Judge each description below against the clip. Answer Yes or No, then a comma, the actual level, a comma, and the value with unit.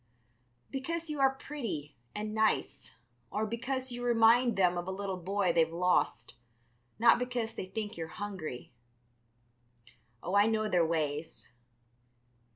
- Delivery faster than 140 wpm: No, slow, 135 wpm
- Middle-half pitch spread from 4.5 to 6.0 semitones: Yes, wide, 5.5 semitones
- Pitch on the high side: Yes, high, 205 Hz